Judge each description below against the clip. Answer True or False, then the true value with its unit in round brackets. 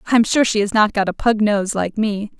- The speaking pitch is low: False (210 Hz)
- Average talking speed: False (275 wpm)